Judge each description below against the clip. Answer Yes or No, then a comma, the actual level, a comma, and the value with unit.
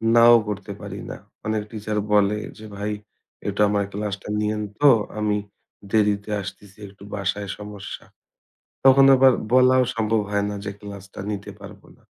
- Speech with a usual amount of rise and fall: No, narrow, 1.2 semitones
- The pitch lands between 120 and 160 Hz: No, low, 105 Hz